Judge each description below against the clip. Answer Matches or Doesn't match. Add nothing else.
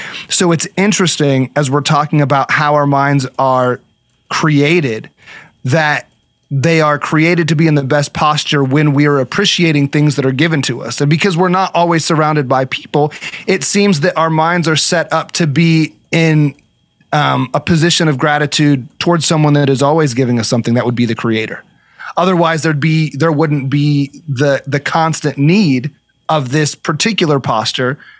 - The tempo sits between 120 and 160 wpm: Doesn't match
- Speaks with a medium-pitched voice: Matches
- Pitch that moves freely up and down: Doesn't match